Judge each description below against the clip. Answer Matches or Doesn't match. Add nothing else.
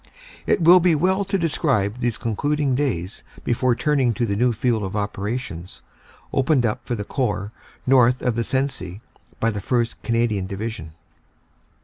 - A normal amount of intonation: Matches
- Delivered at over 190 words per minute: Doesn't match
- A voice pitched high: Doesn't match